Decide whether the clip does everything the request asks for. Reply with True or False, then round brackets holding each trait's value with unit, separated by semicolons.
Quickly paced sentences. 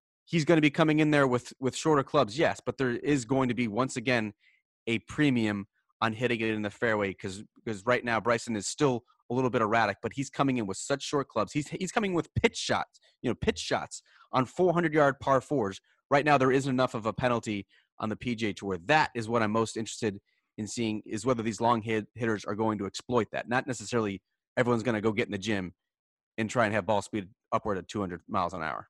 True (240 wpm)